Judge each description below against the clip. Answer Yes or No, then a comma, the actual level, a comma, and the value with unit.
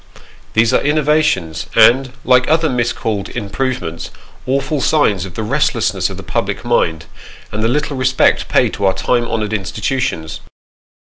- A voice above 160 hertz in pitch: No, low, 120 Hz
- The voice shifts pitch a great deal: No, average, 4.9 semitones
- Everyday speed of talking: Yes, average, 145 wpm